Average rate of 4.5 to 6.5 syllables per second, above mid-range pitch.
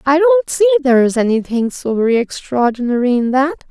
Yes: 5.4 syllables/s; very high, 275 Hz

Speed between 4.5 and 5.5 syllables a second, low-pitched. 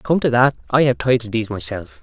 Yes: 5.4 syllables/s; low, 120 Hz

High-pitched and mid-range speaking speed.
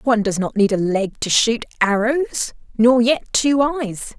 Yes: high, 230 Hz; average, 185 wpm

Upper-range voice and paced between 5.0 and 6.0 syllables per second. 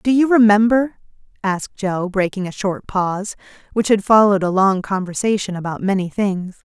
Yes: high, 200 Hz; 5.2 syllables/s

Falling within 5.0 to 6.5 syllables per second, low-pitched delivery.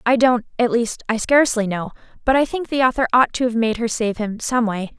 No: 5.8 syllables/s; high, 235 Hz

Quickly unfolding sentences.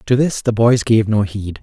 Yes: fast, 260 wpm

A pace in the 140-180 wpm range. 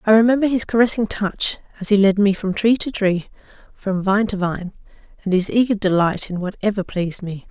No: average, 200 wpm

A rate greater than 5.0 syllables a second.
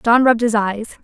Yes: 6.2 syllables/s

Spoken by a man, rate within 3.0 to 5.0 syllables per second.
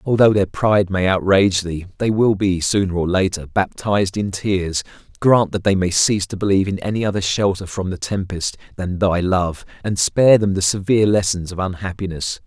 No: male; 5.4 syllables/s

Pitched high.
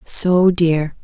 No: medium, 170 Hz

